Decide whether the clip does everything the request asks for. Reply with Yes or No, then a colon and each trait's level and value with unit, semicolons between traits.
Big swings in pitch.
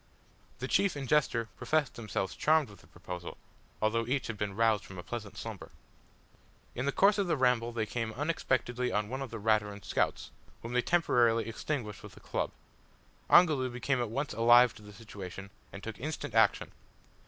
No: average, 4.0 semitones